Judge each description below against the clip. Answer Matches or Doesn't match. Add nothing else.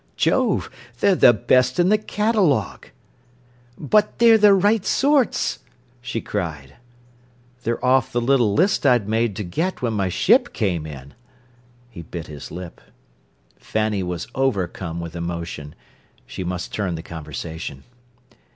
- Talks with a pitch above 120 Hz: Doesn't match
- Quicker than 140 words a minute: Doesn't match